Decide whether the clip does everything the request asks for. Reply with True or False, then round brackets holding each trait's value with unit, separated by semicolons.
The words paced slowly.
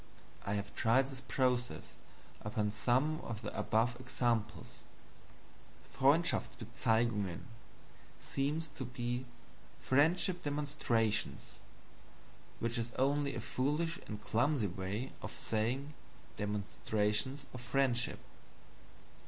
True (95 wpm)